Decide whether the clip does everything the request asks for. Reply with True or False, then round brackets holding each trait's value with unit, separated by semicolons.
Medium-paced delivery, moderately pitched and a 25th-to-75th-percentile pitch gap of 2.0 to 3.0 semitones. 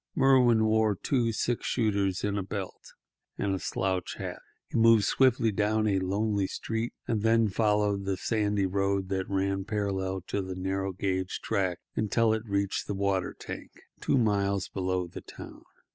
False (165 wpm; 100 Hz; 2.4 semitones)